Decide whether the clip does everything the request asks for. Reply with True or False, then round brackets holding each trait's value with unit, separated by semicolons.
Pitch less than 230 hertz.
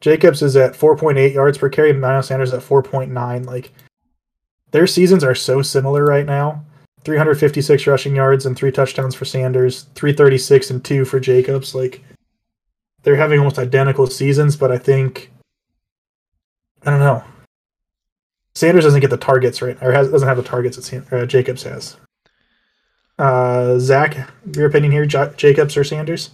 True (135 Hz)